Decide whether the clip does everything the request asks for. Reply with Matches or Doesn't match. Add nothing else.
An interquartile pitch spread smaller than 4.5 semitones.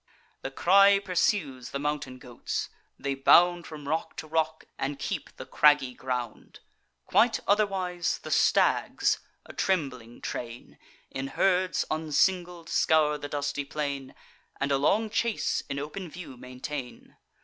Doesn't match